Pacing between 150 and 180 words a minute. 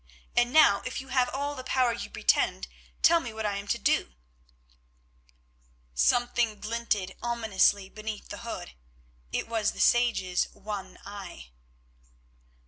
No: slow, 135 wpm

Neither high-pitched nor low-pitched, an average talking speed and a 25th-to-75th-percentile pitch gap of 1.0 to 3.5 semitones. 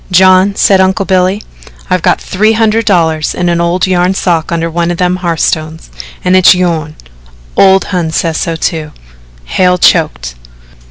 Yes: medium, 180 Hz; average, 160 wpm; narrow, 2.4 semitones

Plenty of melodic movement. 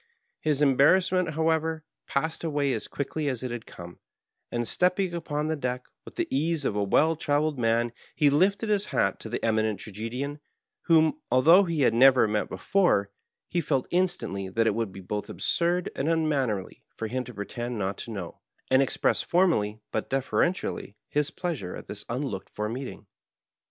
Yes: wide, 6.3 semitones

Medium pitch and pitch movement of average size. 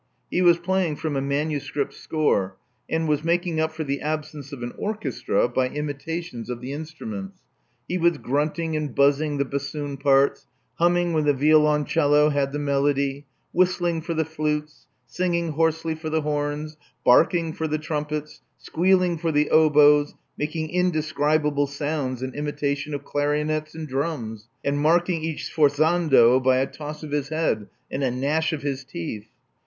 No: medium, 150 Hz; narrow, 2.2 semitones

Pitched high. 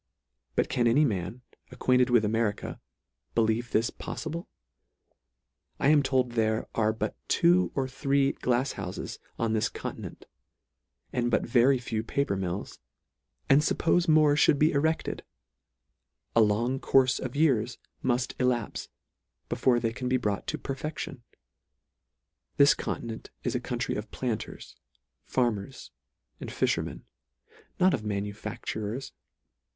No: low, 125 Hz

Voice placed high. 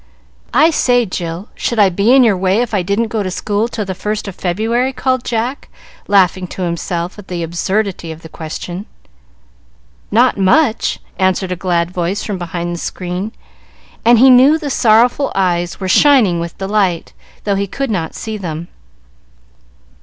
Yes: high, 195 Hz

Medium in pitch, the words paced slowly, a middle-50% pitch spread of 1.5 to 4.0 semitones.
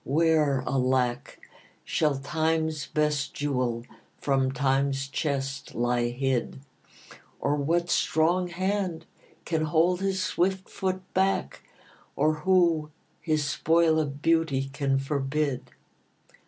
Yes: medium, 150 Hz; slow, 105 wpm; average, 3.5 semitones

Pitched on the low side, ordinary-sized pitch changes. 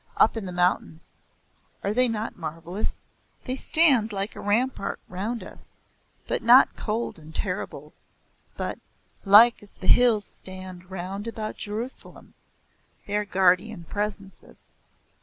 No: high, 205 Hz; average, 3.4 semitones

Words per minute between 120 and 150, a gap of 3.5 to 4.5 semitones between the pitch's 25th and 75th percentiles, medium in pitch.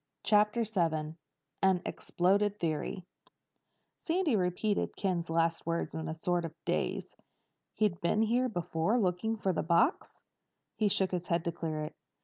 Yes: average, 145 wpm; average, 4.0 semitones; medium, 180 Hz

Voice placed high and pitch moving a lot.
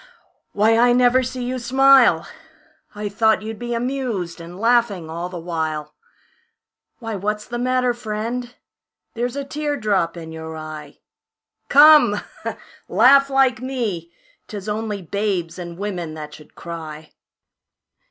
Yes: high, 215 Hz; wide, 6.4 semitones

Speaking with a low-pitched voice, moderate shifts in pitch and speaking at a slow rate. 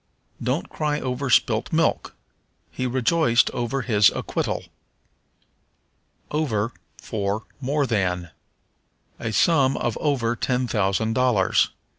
Yes: low, 120 Hz; average, 3.8 semitones; slow, 105 wpm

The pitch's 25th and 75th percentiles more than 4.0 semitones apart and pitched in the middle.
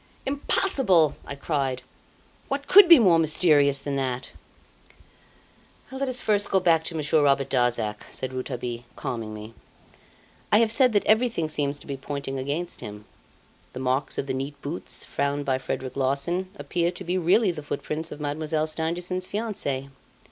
Yes: average, 5.3 semitones; medium, 150 Hz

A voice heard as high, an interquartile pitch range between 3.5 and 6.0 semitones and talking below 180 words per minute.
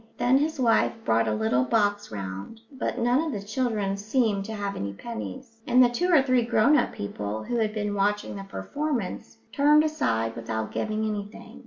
No: high, 215 Hz; average, 4.5 semitones; average, 190 wpm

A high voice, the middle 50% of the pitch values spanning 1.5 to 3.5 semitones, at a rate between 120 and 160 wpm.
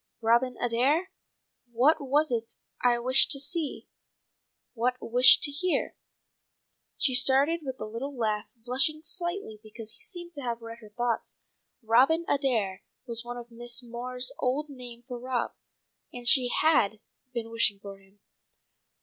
Yes: high, 245 Hz; average, 3.2 semitones; average, 150 wpm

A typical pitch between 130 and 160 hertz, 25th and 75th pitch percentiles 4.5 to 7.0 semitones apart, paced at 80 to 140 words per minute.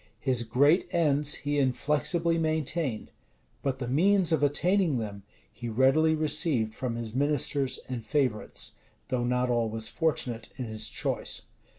Yes: low, 135 Hz; average, 4.8 semitones; slow, 135 wpm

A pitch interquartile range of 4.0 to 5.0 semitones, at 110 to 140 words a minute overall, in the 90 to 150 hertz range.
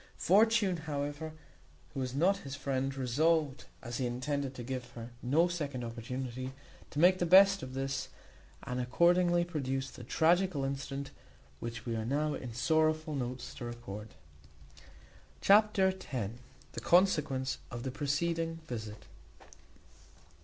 Yes: average, 4.7 semitones; slow, 135 wpm; medium, 140 Hz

